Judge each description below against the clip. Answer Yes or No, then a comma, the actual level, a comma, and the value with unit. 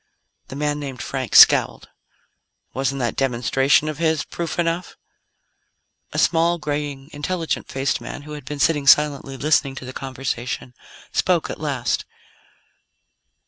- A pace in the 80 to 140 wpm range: Yes, slow, 135 wpm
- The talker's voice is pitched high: No, medium, 145 Hz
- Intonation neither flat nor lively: No, narrow, 2.3 semitones